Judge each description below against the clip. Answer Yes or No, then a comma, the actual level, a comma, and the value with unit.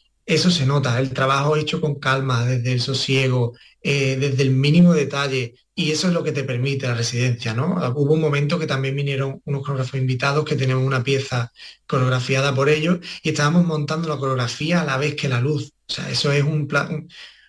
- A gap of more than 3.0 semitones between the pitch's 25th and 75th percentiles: No, narrow, 2.5 semitones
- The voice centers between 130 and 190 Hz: Yes, medium, 140 Hz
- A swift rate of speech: Yes, fast, 200 wpm